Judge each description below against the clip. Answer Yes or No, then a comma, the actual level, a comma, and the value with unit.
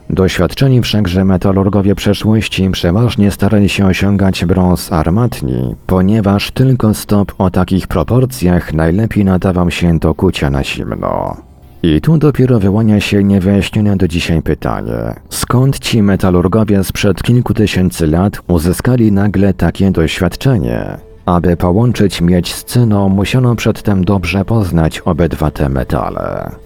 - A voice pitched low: Yes, very low, 95 Hz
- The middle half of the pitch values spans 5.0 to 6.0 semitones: No, average, 3.0 semitones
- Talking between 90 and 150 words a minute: Yes, average, 125 wpm